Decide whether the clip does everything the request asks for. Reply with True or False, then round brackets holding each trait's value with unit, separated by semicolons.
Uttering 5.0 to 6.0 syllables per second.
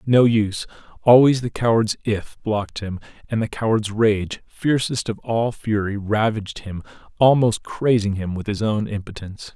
False (4.8 syllables/s)